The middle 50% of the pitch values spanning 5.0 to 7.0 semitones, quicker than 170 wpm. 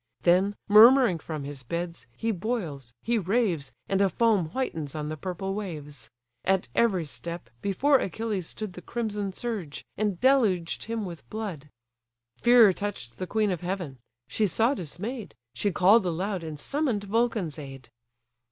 No: average, 5.3 semitones; average, 150 wpm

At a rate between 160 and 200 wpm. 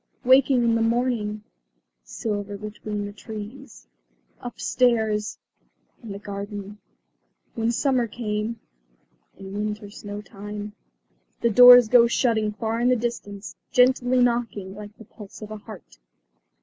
No: average, 145 wpm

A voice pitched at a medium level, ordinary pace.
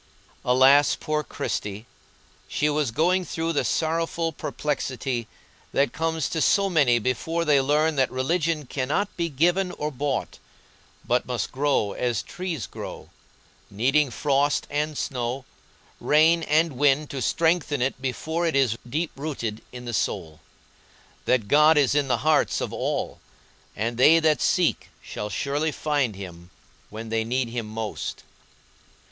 Yes: medium, 145 Hz; average, 145 wpm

